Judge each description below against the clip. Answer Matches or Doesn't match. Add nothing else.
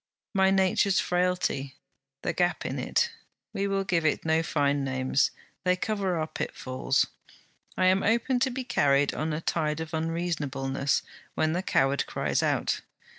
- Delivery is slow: Doesn't match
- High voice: Doesn't match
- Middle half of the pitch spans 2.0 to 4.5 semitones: Doesn't match